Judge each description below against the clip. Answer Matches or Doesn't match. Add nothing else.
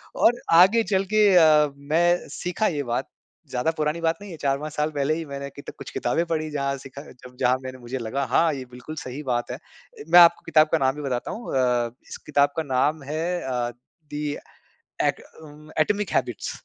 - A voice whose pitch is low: Doesn't match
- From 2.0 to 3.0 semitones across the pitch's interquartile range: Doesn't match